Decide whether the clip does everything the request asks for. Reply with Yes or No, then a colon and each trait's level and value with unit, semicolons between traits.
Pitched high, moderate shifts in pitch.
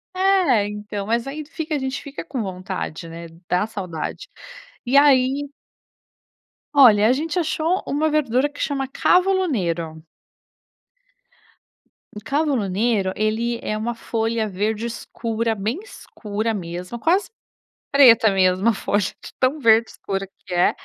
No: high, 230 Hz; wide, 5.8 semitones